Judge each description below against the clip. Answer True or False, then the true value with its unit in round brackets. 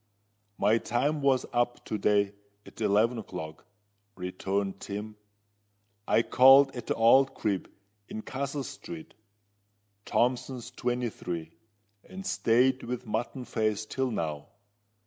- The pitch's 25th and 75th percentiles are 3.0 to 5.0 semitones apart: True (3.9 semitones)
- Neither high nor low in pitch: False (115 Hz)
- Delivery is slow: True (115 wpm)